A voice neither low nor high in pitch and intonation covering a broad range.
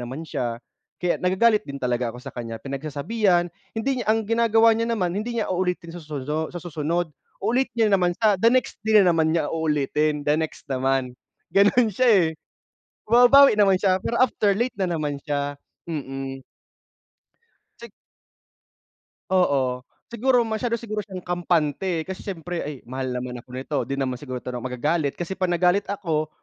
Yes: medium, 175 Hz; wide, 6.8 semitones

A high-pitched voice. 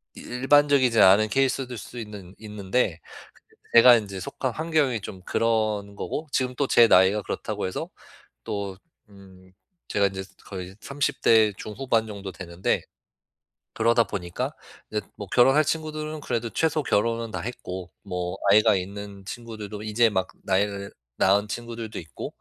No: low, 110 Hz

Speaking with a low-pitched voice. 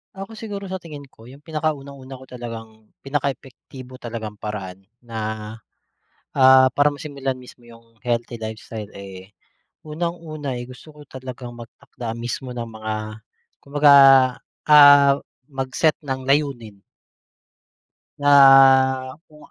Yes: low, 130 Hz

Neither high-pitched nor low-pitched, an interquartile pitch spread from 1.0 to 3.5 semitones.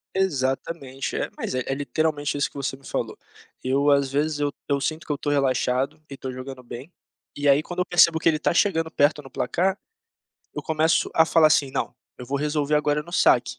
Yes: medium, 145 Hz; average, 2.8 semitones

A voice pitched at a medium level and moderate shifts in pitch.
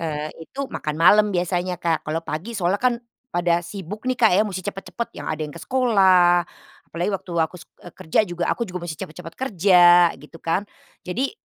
Yes: medium, 175 Hz; average, 3.5 semitones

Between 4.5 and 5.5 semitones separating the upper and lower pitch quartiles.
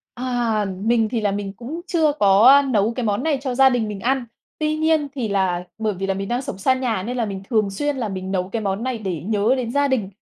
Yes: average, 4.8 semitones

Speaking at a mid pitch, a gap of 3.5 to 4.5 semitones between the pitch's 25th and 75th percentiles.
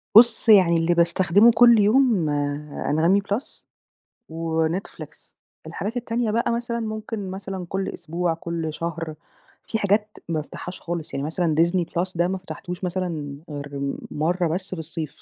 Yes: medium, 180 Hz; average, 4.0 semitones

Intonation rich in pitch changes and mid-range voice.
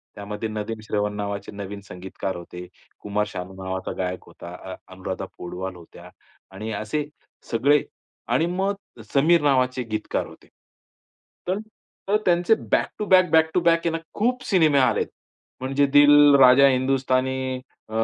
No: wide, 6.5 semitones; low, 130 Hz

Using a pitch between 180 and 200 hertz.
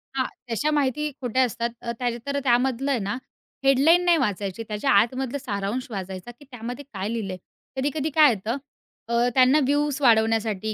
No: high, 245 Hz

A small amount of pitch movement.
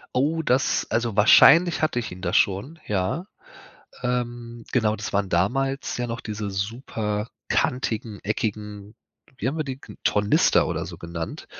No: average, 4.0 semitones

